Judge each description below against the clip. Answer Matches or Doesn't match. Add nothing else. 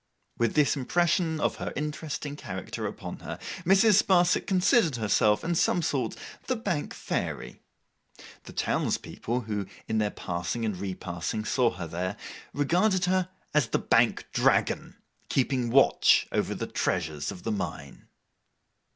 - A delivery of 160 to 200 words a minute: Doesn't match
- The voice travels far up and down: Matches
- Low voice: Matches